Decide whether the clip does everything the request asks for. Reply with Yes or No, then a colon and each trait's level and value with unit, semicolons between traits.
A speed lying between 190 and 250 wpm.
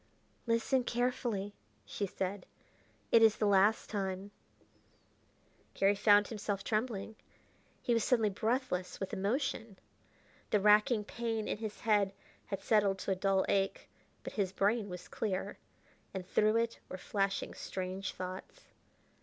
No: slow, 135 wpm